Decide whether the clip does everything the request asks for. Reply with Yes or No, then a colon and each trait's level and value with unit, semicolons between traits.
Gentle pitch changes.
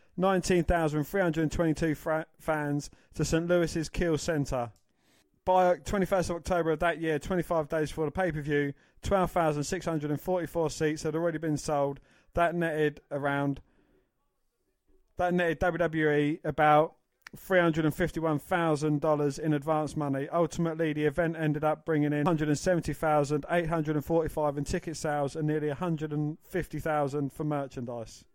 Yes: narrow, 2.3 semitones